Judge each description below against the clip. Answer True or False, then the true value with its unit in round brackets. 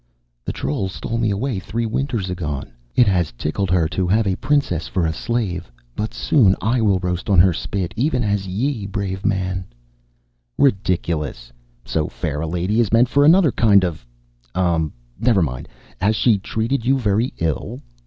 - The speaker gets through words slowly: False (175 wpm)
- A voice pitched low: True (95 Hz)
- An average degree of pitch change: True (4.7 semitones)